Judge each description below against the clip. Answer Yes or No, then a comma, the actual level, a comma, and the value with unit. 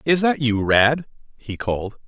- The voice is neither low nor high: No, low, 125 Hz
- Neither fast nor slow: Yes, average, 175 wpm